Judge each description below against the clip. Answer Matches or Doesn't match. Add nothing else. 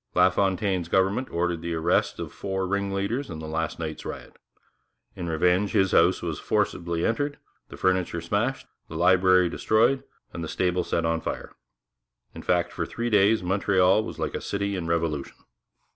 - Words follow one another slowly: Doesn't match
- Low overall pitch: Matches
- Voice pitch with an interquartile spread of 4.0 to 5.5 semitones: Doesn't match